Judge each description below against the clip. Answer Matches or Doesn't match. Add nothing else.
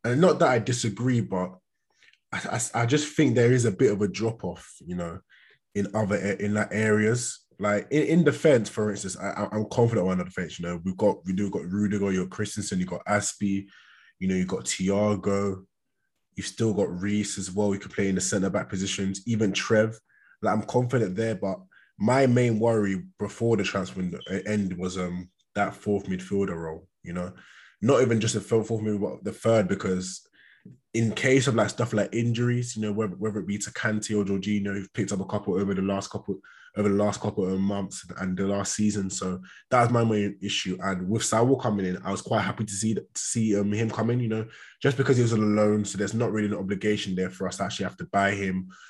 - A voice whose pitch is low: Matches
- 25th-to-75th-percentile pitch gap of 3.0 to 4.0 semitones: Doesn't match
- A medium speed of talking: Doesn't match